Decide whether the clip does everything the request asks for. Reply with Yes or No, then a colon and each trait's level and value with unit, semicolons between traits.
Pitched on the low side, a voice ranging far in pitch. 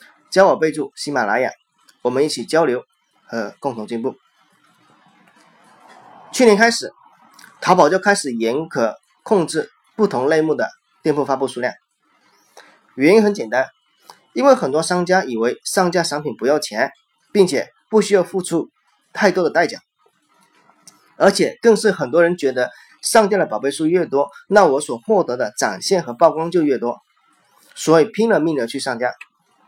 No: medium, 165 Hz; wide, 6.7 semitones